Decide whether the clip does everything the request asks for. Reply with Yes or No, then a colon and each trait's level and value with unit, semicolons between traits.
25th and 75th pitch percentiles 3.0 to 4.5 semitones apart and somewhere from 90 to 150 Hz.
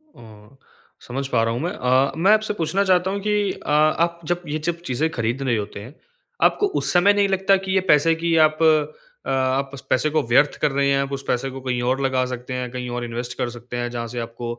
No: wide, 5.6 semitones; low, 135 Hz